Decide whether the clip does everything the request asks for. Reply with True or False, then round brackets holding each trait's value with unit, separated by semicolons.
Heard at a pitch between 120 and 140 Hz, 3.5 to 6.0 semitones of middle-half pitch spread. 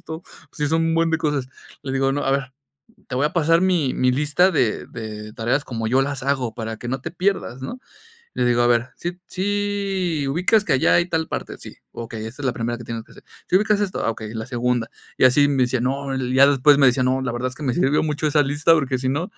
True (135 Hz; 4.6 semitones)